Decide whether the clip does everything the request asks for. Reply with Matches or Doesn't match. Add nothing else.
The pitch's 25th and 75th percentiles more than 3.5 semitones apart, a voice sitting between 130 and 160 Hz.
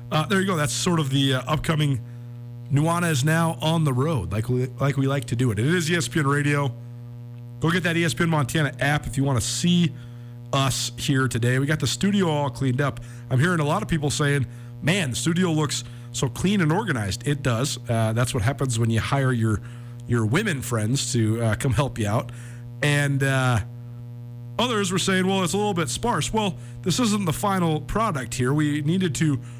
Matches